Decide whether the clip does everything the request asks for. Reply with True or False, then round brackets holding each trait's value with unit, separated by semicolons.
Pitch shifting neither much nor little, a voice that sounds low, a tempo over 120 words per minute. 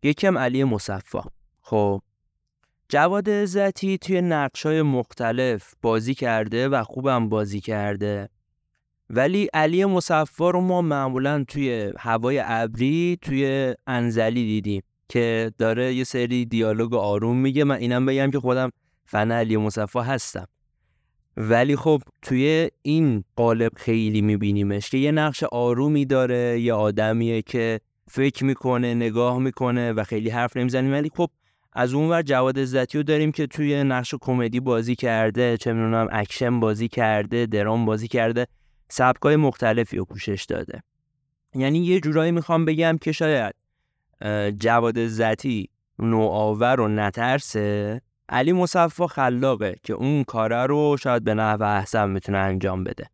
True (4.1 semitones; 125 Hz; 135 wpm)